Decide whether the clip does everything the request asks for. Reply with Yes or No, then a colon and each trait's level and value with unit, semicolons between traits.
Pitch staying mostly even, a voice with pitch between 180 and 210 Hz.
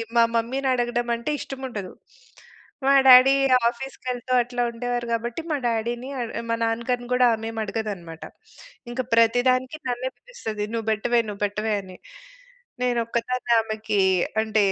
No: narrow, 2.2 semitones; high, 235 Hz